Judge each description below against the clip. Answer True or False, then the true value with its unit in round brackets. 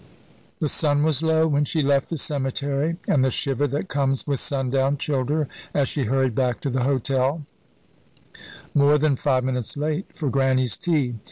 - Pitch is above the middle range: False (140 Hz)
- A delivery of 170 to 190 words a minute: True (175 wpm)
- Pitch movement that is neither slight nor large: False (2.1 semitones)